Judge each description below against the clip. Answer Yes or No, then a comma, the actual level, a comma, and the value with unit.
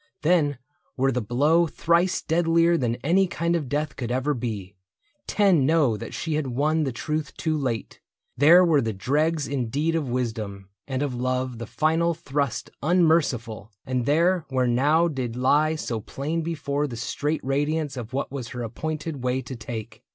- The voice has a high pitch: No, medium, 140 Hz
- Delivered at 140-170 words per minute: No, average, 180 wpm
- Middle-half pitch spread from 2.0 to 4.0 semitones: No, average, 4.4 semitones